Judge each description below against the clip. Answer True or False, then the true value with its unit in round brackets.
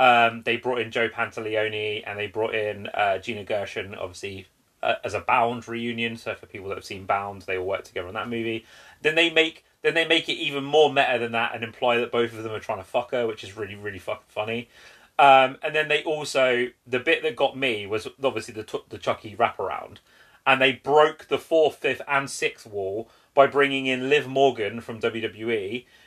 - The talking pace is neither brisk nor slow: False (220 wpm)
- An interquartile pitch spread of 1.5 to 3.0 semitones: False (3.9 semitones)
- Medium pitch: False (120 Hz)